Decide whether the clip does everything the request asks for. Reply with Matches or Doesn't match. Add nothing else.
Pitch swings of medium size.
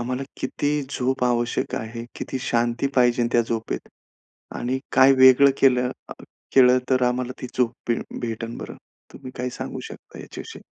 Doesn't match